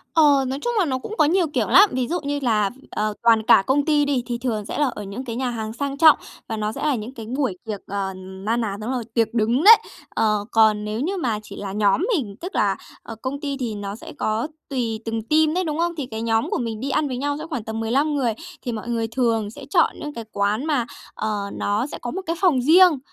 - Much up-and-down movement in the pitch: No, average, 4.9 semitones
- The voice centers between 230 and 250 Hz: Yes, high, 240 Hz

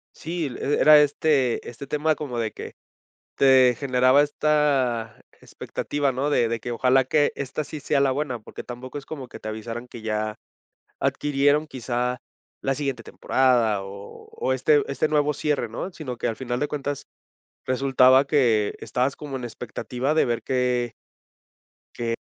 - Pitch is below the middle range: Yes, low, 130 Hz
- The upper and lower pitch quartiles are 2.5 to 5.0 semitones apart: Yes, average, 3.3 semitones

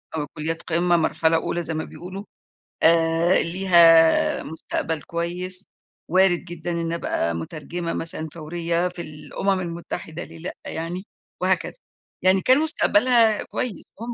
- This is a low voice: No, medium, 170 Hz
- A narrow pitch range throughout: Yes, narrow, 2.2 semitones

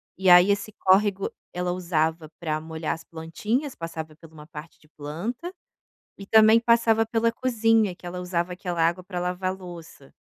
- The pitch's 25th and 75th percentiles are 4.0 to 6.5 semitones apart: Yes, average, 4.7 semitones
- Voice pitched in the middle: Yes, medium, 180 Hz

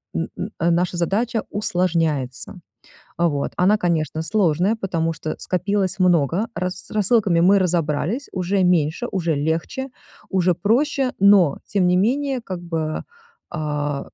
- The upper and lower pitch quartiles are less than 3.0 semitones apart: No, average, 3.8 semitones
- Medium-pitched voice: Yes, medium, 180 Hz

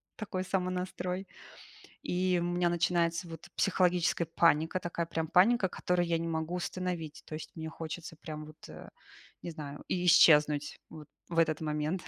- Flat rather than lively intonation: Yes, narrow, 2.1 semitones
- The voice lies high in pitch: No, medium, 170 Hz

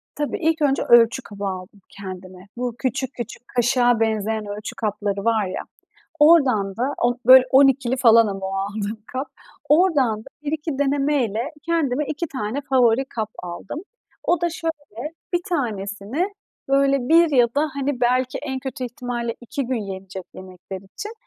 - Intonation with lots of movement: No, average, 4.9 semitones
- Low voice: No, high, 245 Hz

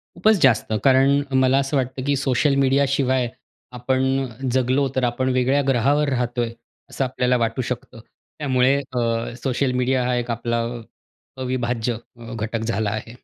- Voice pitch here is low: Yes, low, 130 Hz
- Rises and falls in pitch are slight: Yes, narrow, 2.1 semitones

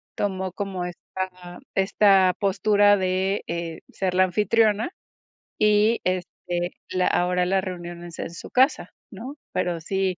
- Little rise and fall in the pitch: Yes, narrow, 2.3 semitones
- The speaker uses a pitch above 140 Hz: Yes, medium, 185 Hz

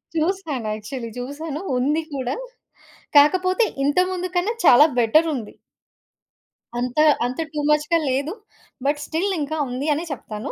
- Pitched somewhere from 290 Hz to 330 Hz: Yes, very high, 295 Hz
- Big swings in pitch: No, average, 4.6 semitones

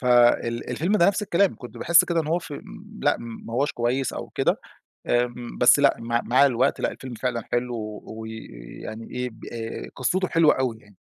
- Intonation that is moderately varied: Yes, average, 3.7 semitones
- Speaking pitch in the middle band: No, low, 125 Hz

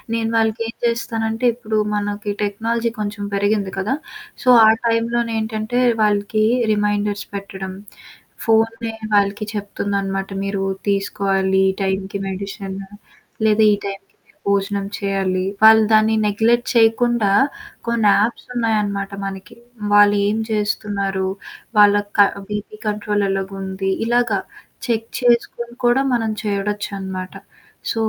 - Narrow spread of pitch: Yes, narrow, 2.1 semitones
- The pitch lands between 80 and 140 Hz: No, high, 205 Hz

